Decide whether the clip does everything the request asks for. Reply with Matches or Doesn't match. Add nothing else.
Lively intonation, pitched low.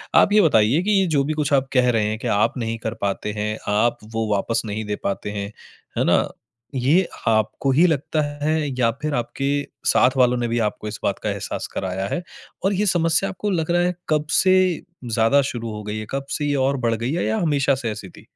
Matches